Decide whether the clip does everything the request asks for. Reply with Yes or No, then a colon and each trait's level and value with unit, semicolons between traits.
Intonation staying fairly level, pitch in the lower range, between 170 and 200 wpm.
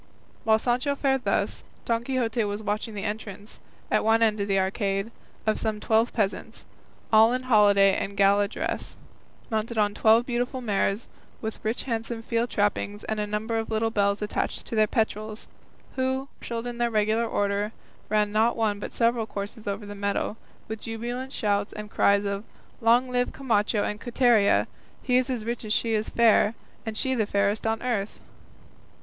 No: narrow, 2.3 semitones; high, 220 Hz; average, 175 wpm